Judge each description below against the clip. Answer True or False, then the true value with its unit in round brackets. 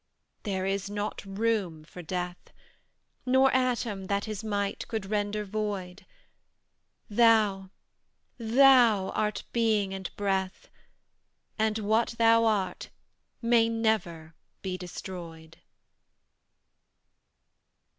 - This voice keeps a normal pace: False (95 wpm)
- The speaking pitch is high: True (205 Hz)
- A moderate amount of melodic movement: True (3.0 semitones)